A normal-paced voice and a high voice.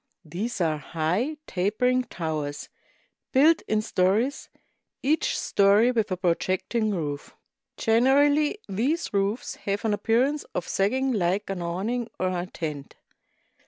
No: slow, 125 wpm; high, 205 Hz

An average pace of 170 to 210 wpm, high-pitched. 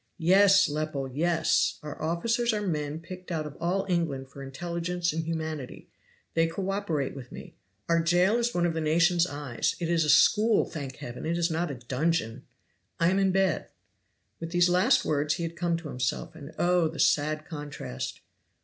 No: average, 185 wpm; medium, 165 Hz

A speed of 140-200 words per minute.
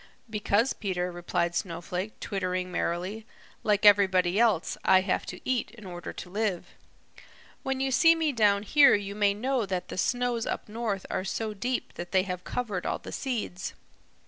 Yes: average, 170 wpm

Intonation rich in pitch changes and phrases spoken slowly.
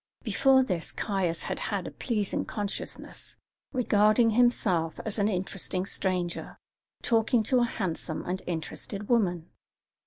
No: average, 4.2 semitones; slow, 125 wpm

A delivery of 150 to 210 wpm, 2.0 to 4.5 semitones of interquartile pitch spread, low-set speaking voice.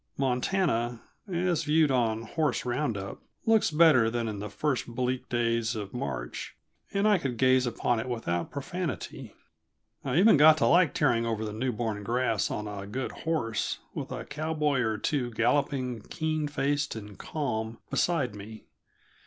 No: average, 160 wpm; average, 5.1 semitones; low, 125 Hz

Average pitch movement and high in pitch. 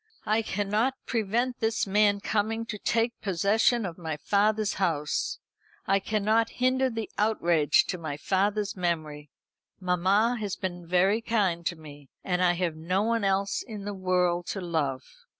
Yes: average, 3.8 semitones; high, 195 Hz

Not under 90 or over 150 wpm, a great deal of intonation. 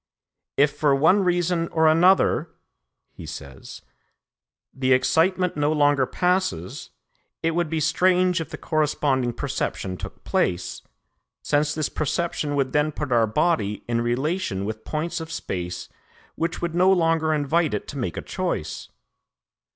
No: average, 145 wpm; average, 4.5 semitones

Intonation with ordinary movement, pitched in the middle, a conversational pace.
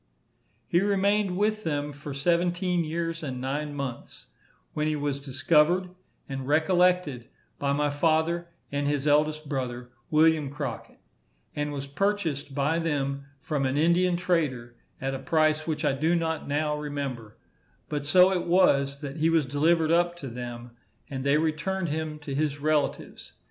Yes: average, 3.1 semitones; medium, 150 Hz; average, 155 wpm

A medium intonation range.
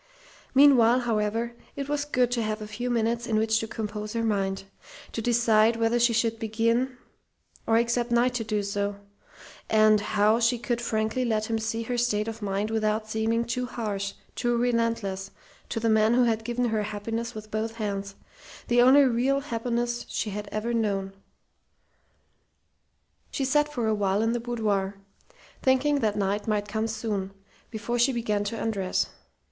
No: narrow, 2.0 semitones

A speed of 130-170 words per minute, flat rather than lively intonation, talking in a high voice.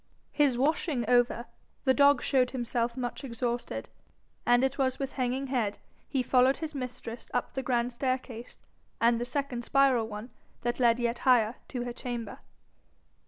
Yes: average, 160 wpm; narrow, 1.9 semitones; very high, 250 Hz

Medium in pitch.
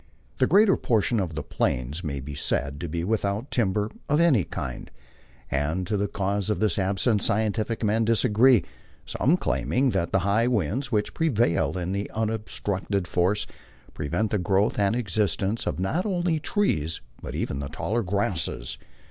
No: low, 105 Hz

